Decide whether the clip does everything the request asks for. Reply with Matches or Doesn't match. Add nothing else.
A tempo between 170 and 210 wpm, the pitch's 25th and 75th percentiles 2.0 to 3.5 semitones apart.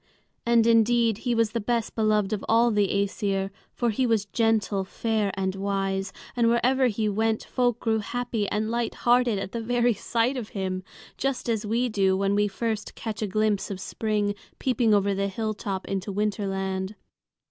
Matches